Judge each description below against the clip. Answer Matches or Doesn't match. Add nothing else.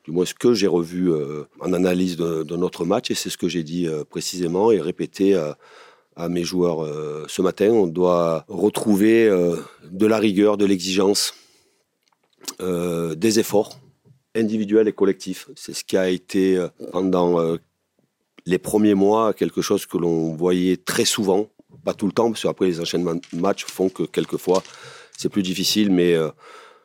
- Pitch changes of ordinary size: Matches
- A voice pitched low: Matches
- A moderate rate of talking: Matches